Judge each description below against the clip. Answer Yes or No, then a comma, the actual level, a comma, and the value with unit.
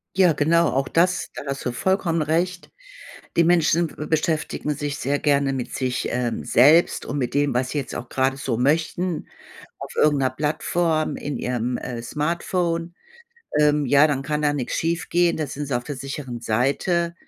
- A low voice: No, medium, 145 Hz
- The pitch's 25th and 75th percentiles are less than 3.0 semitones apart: No, average, 3.9 semitones